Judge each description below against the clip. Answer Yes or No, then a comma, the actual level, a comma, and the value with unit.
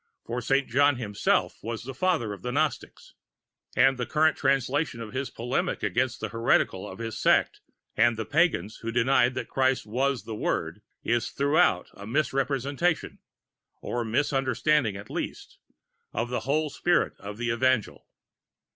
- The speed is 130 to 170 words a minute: Yes, average, 155 wpm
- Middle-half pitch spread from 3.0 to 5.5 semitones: Yes, average, 3.4 semitones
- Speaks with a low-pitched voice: Yes, low, 125 Hz